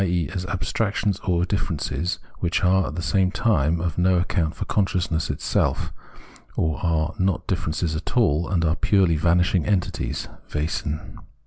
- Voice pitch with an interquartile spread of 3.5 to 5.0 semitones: No, average, 2.9 semitones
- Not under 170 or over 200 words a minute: No, average, 150 wpm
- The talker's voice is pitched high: No, very low, 85 Hz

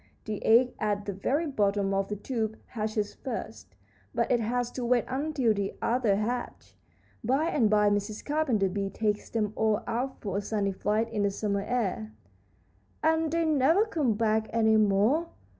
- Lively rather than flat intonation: No, average, 3.7 semitones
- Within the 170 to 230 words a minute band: Yes, average, 175 wpm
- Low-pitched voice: No, high, 220 Hz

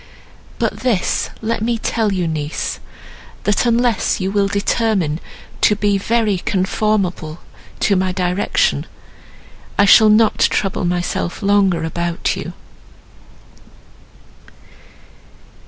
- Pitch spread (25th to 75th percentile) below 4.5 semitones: Yes, average, 3.3 semitones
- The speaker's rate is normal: No, slow, 105 wpm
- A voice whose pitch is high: Yes, high, 200 Hz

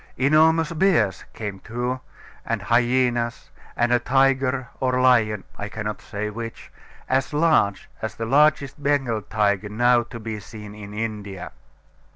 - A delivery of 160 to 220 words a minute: No, average, 140 wpm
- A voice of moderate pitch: No, low, 120 Hz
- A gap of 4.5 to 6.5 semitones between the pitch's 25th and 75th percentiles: No, average, 3.8 semitones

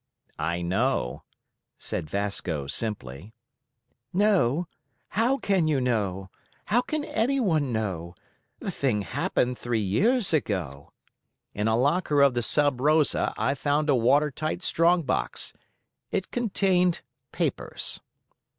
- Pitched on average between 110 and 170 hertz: Yes, low, 135 Hz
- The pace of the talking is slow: Yes, slow, 120 wpm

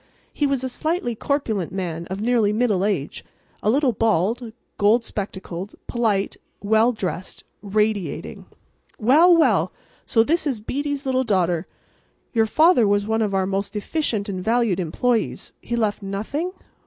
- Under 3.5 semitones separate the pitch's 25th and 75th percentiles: No, average, 4.0 semitones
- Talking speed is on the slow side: No, average, 150 wpm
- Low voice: No, high, 220 Hz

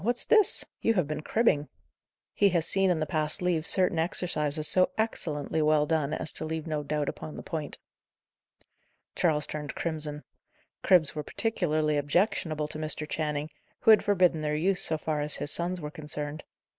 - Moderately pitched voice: Yes, medium, 155 Hz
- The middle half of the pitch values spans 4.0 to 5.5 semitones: No, average, 3.0 semitones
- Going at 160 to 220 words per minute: Yes, average, 175 wpm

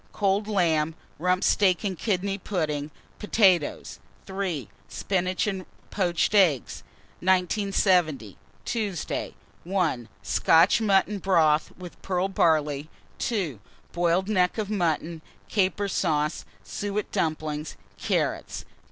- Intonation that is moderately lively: Yes, average, 3.7 semitones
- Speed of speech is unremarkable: No, slow, 100 wpm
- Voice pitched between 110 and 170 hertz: No, medium, 180 Hz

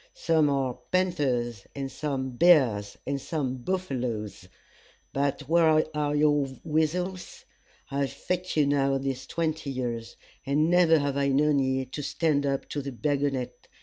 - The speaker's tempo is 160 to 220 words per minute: No, average, 150 wpm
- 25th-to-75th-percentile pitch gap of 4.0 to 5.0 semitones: No, average, 2.9 semitones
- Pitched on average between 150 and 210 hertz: No, medium, 140 Hz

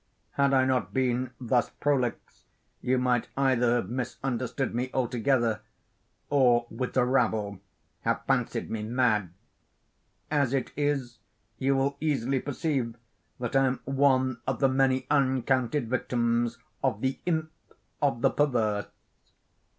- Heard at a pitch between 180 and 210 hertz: No, low, 130 Hz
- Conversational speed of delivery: No, slow, 130 wpm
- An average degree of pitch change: No, narrow, 2.2 semitones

